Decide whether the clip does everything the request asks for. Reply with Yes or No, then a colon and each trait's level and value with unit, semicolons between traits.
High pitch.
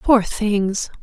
Yes: high, 210 Hz